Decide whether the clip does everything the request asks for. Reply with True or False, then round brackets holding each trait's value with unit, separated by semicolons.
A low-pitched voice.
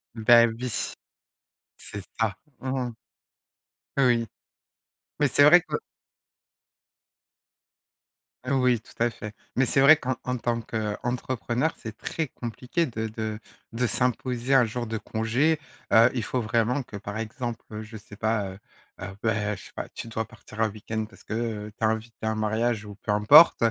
True (115 Hz)